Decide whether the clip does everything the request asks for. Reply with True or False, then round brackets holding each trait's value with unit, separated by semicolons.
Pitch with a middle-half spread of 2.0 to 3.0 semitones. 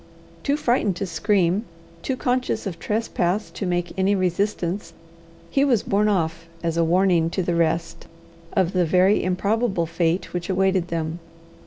False (3.4 semitones)